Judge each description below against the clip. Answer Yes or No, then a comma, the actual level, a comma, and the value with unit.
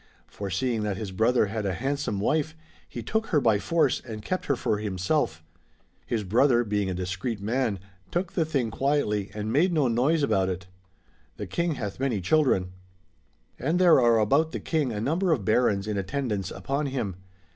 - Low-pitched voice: Yes, low, 120 Hz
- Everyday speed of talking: Yes, average, 185 wpm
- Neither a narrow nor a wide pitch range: No, wide, 6.1 semitones